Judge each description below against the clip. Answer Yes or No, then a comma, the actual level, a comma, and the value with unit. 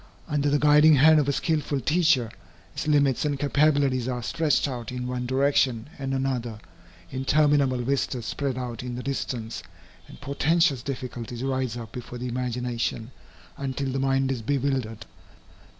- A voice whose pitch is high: No, low, 135 Hz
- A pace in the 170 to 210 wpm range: No, average, 150 wpm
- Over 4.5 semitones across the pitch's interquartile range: No, narrow, 2.5 semitones